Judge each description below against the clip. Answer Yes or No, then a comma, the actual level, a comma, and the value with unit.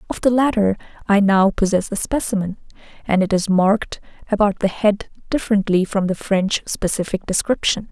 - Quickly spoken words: No, average, 160 wpm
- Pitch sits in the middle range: No, high, 200 Hz